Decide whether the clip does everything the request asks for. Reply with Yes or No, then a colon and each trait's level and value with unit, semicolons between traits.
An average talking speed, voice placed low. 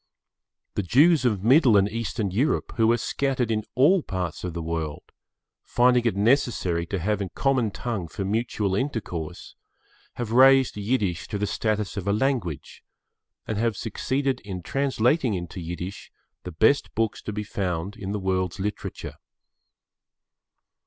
Yes: average, 150 wpm; low, 105 Hz